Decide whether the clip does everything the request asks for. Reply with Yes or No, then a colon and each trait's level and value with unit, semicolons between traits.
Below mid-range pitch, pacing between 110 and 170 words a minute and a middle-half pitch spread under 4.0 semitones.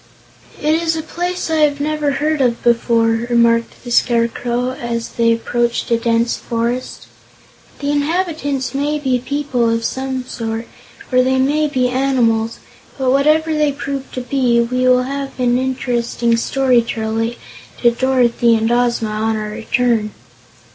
No: very high, 250 Hz; average, 155 wpm; average, 3.1 semitones